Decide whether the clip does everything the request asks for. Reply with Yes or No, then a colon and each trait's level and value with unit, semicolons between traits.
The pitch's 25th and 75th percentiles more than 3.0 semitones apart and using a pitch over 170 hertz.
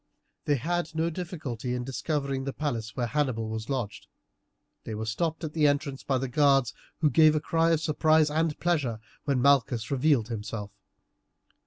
No: average, 4.4 semitones; medium, 140 Hz